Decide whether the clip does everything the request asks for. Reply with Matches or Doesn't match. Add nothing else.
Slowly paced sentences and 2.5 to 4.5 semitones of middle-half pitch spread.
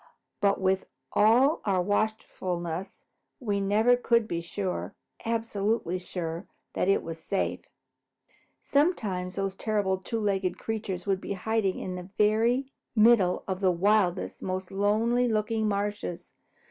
Matches